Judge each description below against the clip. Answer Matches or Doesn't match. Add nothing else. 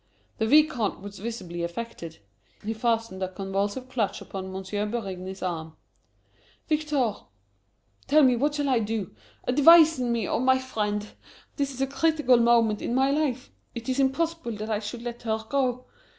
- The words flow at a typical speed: Matches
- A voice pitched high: Matches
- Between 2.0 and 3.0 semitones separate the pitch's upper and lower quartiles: Doesn't match